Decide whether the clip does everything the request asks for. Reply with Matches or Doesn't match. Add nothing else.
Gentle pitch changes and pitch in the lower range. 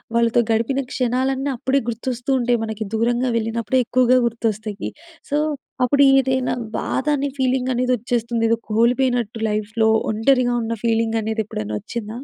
Doesn't match